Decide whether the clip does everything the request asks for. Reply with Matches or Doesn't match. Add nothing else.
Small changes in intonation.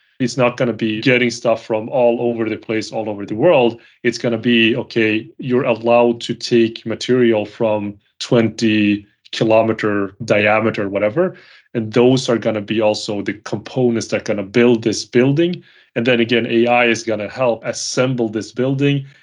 Matches